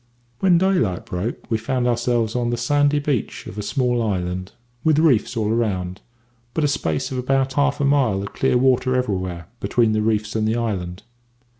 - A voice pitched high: No, low, 120 Hz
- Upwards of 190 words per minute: Yes, fast, 205 wpm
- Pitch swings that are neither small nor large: Yes, average, 4.5 semitones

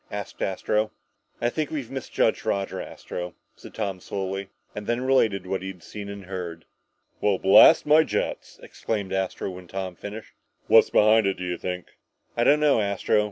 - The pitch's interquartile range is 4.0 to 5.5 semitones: No, average, 2.9 semitones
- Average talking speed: Yes, average, 180 wpm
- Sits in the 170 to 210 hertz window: No, low, 100 Hz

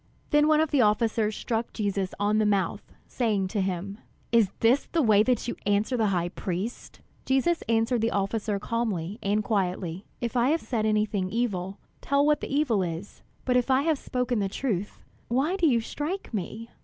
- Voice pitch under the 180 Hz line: No, high, 220 Hz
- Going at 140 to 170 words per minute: No, average, 190 wpm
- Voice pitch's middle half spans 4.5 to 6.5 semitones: No, average, 4.0 semitones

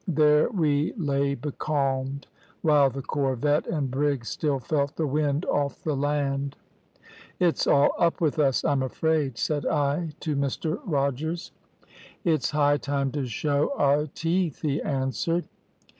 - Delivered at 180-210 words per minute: No, average, 140 wpm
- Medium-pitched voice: Yes, medium, 145 Hz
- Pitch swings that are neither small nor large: No, narrow, 2.0 semitones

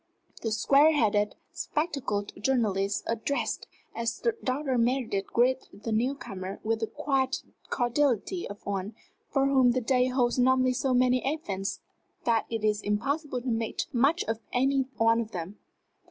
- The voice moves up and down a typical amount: Yes, average, 3.7 semitones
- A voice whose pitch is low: No, high, 240 Hz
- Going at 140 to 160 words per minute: Yes, average, 150 wpm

